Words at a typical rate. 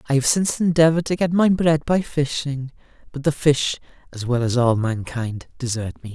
Yes: average, 195 wpm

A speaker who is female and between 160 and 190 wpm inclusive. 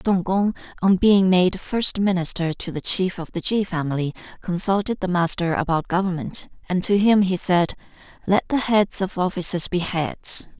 Yes: female; average, 175 wpm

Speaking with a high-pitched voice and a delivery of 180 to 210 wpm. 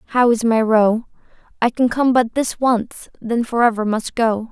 Yes: high, 230 Hz; average, 200 wpm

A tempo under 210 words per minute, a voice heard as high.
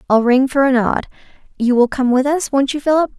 No: fast, 225 wpm; very high, 265 Hz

